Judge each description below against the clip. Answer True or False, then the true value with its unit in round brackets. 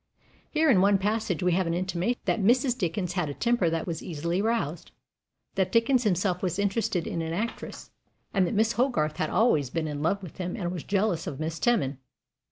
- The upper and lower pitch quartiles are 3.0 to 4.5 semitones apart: False (5.0 semitones)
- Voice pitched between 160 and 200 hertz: True (185 Hz)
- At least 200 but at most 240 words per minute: True (205 wpm)